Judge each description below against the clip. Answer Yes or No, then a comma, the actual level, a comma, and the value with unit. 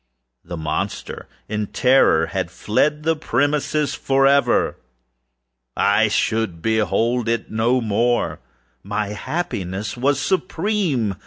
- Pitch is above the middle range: No, low, 115 Hz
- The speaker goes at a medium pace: No, slow, 100 wpm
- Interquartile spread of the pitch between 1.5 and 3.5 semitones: No, wide, 5.6 semitones